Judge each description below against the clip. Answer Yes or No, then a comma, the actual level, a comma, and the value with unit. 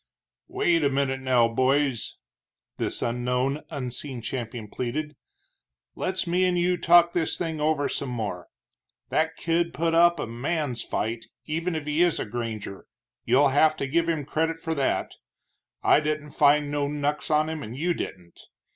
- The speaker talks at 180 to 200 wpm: No, average, 165 wpm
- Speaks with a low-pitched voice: No, medium, 145 Hz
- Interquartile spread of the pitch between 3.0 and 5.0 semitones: Yes, average, 4.5 semitones